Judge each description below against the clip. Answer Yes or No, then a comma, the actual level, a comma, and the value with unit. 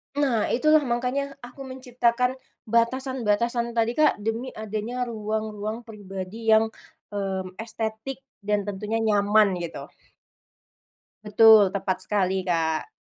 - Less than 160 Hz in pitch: No, high, 220 Hz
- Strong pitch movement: No, average, 2.9 semitones